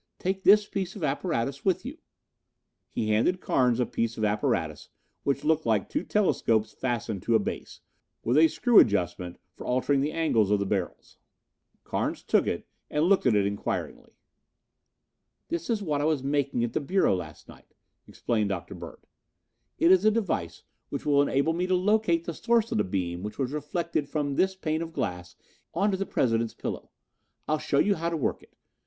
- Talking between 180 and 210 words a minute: Yes, average, 185 wpm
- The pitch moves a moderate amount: No, wide, 8.3 semitones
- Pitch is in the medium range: Yes, medium, 145 Hz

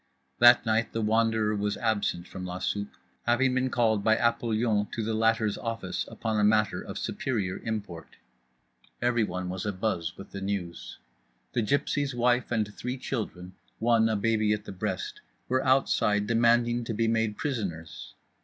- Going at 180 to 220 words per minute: No, average, 160 wpm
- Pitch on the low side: Yes, low, 110 Hz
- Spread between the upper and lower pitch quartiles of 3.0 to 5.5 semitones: No, narrow, 2.5 semitones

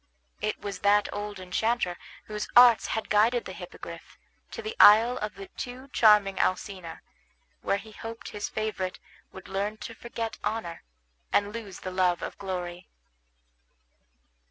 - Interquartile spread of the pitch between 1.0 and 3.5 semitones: Yes, average, 3.0 semitones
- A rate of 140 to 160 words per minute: Yes, average, 145 wpm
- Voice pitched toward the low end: No, high, 210 Hz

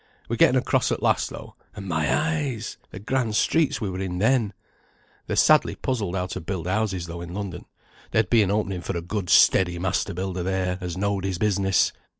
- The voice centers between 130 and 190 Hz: No, very low, 95 Hz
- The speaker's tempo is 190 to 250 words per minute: Yes, average, 200 wpm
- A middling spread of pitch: Yes, average, 3.0 semitones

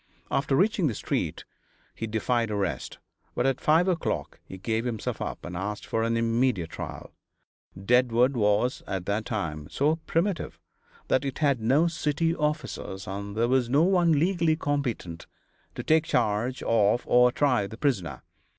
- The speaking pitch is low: Yes, low, 125 Hz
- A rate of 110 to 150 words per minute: No, average, 160 wpm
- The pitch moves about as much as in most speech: No, wide, 6.0 semitones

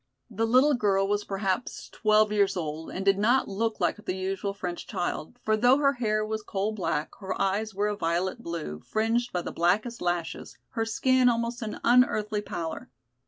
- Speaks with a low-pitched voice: No, high, 210 Hz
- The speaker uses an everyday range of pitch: Yes, average, 3.3 semitones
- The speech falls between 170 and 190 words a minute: Yes, average, 185 wpm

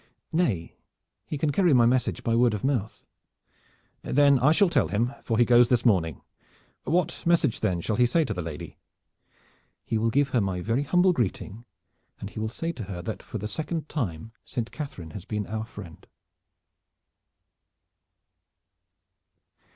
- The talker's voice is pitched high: No, low, 120 Hz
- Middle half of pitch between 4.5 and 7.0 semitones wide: Yes, wide, 5.5 semitones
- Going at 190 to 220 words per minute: No, average, 165 wpm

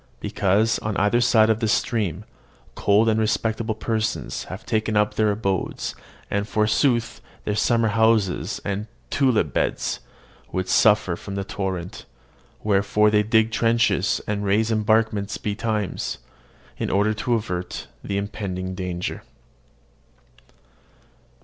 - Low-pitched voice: Yes, low, 105 Hz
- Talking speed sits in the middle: No, slow, 125 wpm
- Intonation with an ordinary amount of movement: No, narrow, 1.9 semitones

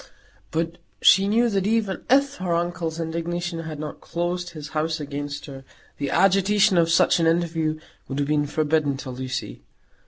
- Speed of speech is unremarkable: Yes, average, 165 wpm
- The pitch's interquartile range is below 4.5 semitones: Yes, average, 3.0 semitones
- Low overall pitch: No, medium, 165 Hz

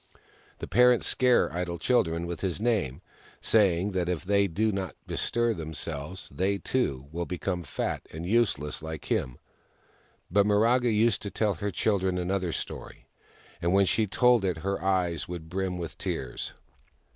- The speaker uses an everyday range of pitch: Yes, average, 3.6 semitones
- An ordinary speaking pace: Yes, average, 155 wpm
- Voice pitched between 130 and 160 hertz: No, very low, 95 Hz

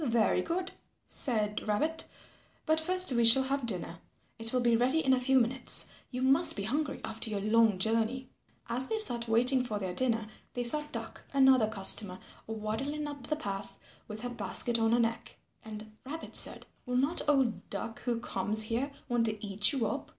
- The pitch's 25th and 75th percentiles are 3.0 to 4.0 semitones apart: Yes, average, 3.5 semitones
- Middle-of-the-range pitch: No, high, 235 Hz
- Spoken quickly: No, average, 185 wpm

